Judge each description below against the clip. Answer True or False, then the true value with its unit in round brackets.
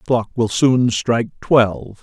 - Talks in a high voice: False (115 Hz)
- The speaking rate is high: False (180 wpm)